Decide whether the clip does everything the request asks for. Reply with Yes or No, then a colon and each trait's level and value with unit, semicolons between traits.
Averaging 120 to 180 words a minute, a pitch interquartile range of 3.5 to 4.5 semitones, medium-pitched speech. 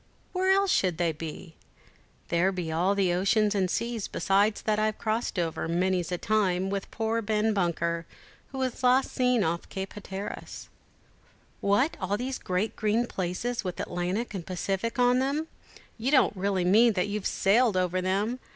No: average, 170 wpm; average, 4.0 semitones; high, 200 Hz